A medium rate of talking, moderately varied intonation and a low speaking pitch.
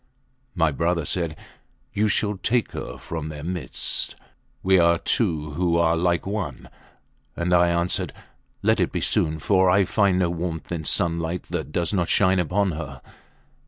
No: average, 160 wpm; narrow, 2.3 semitones; very low, 85 Hz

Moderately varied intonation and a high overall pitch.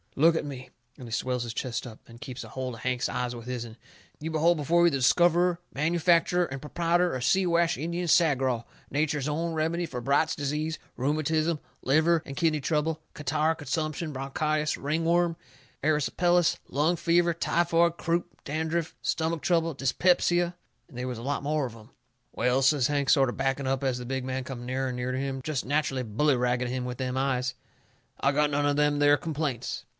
No: average, 4.0 semitones; medium, 145 Hz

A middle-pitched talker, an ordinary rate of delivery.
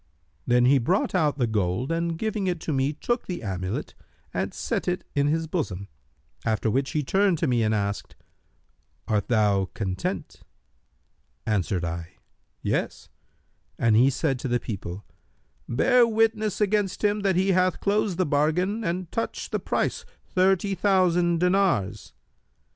Yes: medium, 160 Hz; average, 150 wpm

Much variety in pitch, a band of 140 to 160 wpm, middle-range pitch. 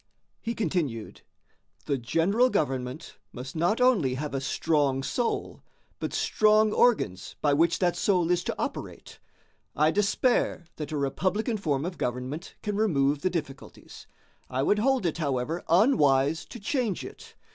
Yes: wide, 7.2 semitones; average, 145 wpm; medium, 165 Hz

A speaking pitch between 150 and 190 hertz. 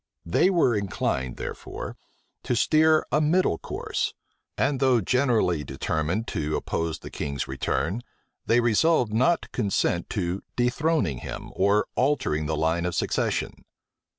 No: low, 105 Hz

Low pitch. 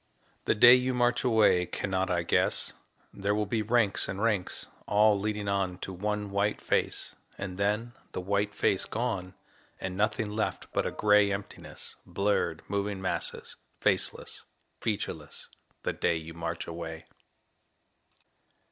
Yes: low, 100 Hz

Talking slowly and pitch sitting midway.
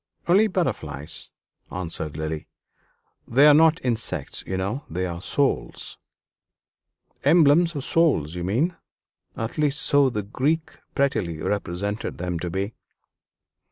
No: slow, 120 wpm; low, 110 Hz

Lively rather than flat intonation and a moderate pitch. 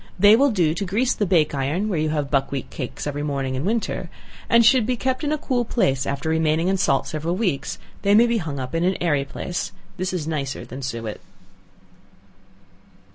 Yes: wide, 7.0 semitones; medium, 165 Hz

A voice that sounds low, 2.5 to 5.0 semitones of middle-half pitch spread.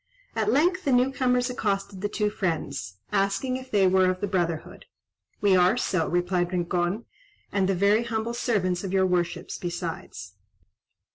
No: high, 195 Hz; average, 4.3 semitones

